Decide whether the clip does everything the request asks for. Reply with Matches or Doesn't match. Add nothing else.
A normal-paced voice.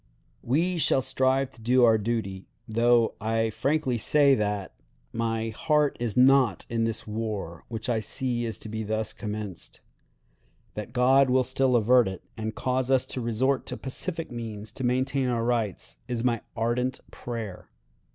Matches